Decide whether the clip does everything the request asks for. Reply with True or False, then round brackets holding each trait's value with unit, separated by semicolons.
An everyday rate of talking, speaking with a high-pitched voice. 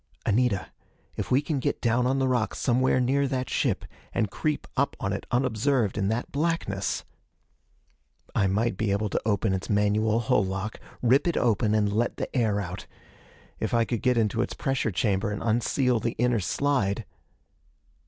False (175 wpm; 115 Hz)